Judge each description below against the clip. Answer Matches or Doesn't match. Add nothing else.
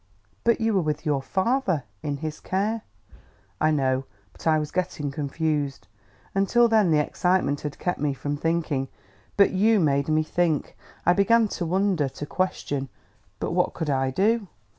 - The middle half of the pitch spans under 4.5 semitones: Doesn't match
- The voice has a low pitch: Doesn't match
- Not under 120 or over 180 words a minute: Matches